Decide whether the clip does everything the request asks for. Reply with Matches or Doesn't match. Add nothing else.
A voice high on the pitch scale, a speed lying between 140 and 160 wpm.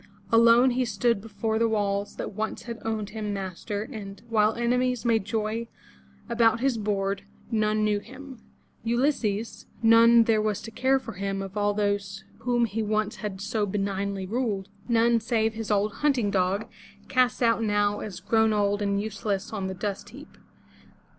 Doesn't match